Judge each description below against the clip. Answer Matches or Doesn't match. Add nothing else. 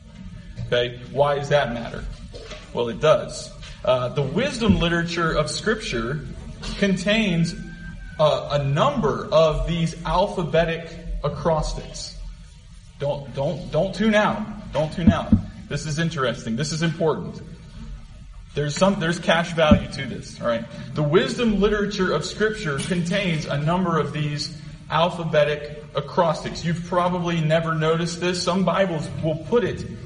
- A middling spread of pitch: Matches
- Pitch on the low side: Doesn't match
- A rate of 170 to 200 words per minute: Doesn't match